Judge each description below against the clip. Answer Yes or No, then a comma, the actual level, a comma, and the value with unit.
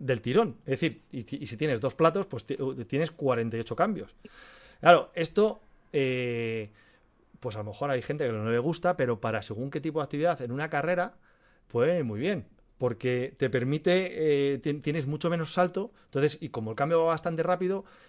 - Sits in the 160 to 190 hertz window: No, medium, 145 Hz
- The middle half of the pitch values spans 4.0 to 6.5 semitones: Yes, average, 5.2 semitones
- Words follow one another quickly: Yes, fast, 195 wpm